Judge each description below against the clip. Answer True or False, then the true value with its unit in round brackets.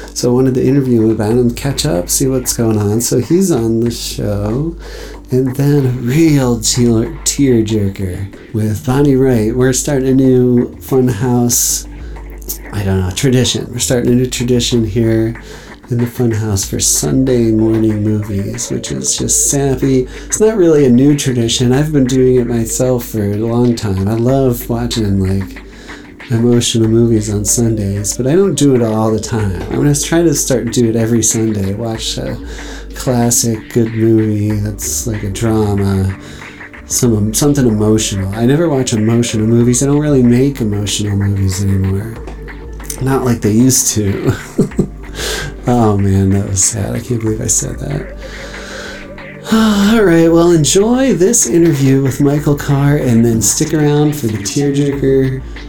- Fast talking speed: False (165 wpm)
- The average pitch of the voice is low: True (120 Hz)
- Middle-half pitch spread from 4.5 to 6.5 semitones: False (3.6 semitones)